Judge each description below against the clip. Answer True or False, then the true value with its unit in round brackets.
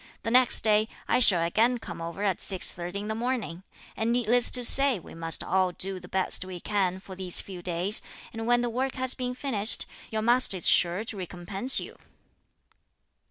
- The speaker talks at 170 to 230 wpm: True (195 wpm)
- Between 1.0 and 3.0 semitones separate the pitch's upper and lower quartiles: False (4.8 semitones)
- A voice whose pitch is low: False (210 Hz)